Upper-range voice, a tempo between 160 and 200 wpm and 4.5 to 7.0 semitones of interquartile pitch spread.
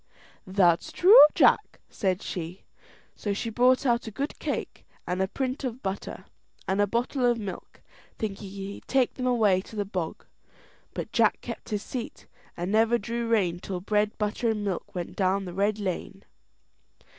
No: high, 205 Hz; average, 170 wpm; average, 3.7 semitones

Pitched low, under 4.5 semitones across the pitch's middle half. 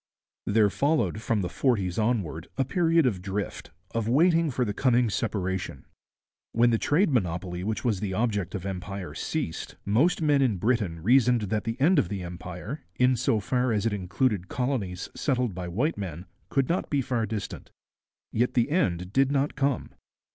No: low, 110 Hz; wide, 5.6 semitones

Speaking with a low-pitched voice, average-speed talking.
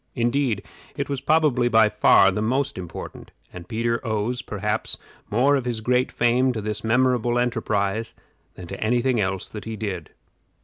Yes: low, 115 Hz; average, 170 wpm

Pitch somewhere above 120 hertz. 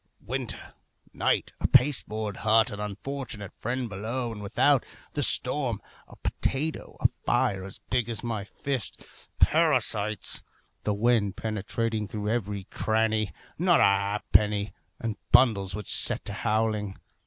No: low, 110 Hz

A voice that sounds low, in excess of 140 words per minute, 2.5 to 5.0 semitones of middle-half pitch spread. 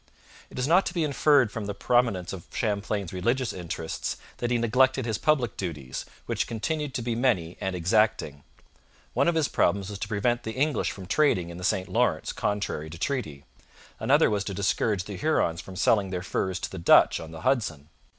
No: low, 105 Hz; average, 200 wpm; wide, 5.4 semitones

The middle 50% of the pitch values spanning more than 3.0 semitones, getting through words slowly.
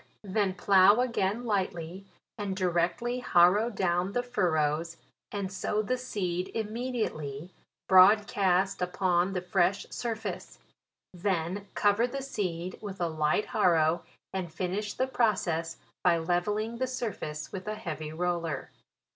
Yes: average, 3.6 semitones; slow, 130 wpm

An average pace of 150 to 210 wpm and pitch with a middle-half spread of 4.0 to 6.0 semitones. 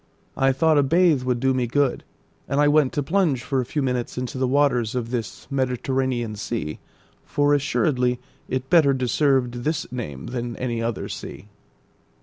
No: average, 170 wpm; average, 2.8 semitones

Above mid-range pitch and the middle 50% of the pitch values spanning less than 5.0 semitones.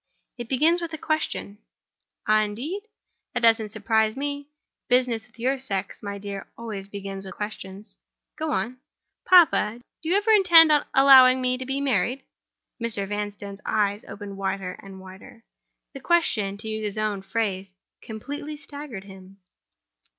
No: high, 220 Hz; average, 5.3 semitones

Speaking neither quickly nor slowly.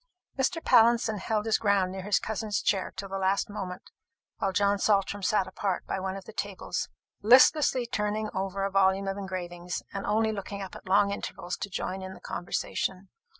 Yes: average, 190 wpm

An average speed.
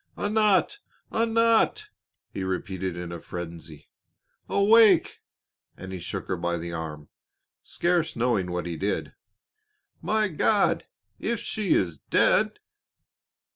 No: slow, 115 wpm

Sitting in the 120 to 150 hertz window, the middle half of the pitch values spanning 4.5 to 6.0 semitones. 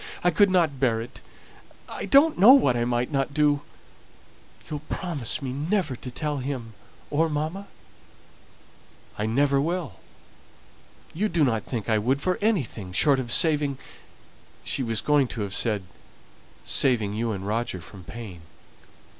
Yes: low, 135 Hz; wide, 5.5 semitones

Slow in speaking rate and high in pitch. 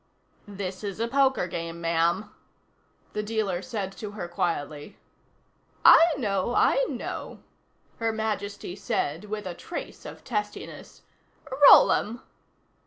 Yes: slow, 120 wpm; high, 205 Hz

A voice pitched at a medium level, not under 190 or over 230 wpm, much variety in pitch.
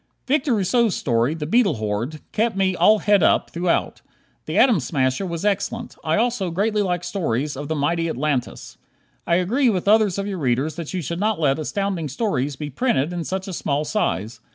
Yes: medium, 175 Hz; average, 195 wpm; wide, 5.8 semitones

